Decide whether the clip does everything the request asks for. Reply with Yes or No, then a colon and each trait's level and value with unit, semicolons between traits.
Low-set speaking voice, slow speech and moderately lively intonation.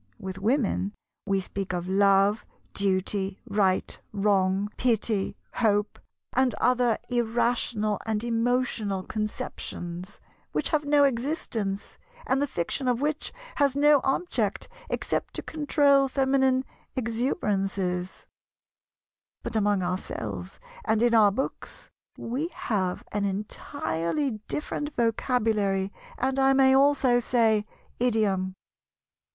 No: high, 225 Hz; slow, 110 wpm; average, 5.0 semitones